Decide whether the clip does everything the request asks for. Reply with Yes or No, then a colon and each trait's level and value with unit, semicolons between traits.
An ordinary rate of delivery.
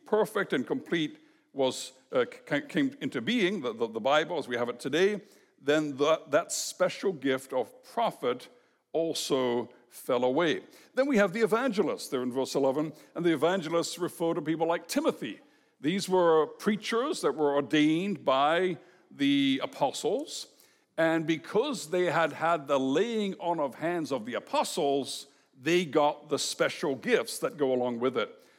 Yes: average, 160 wpm